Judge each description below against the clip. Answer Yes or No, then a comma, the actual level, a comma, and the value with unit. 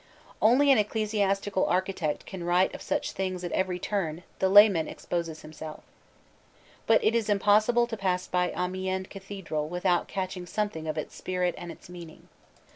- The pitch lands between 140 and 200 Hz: Yes, medium, 185 Hz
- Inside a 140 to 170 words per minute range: Yes, average, 160 wpm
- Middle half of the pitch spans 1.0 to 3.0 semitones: Yes, narrow, 2.6 semitones